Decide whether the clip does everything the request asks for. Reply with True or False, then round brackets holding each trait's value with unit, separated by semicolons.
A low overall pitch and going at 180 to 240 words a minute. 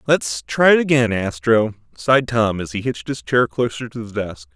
True (115 Hz; 200 wpm)